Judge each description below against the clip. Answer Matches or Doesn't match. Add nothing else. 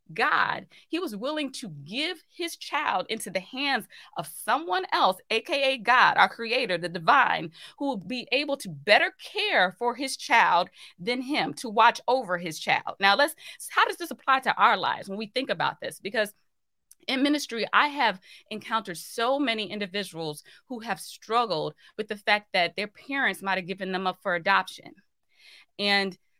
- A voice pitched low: Doesn't match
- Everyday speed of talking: Matches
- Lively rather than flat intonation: Matches